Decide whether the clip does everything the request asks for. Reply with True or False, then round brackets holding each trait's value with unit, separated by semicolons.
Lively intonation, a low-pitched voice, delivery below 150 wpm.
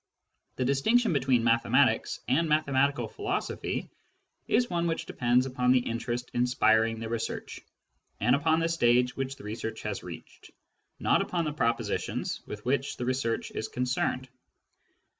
False (4.1 semitones; 130 Hz; 140 wpm)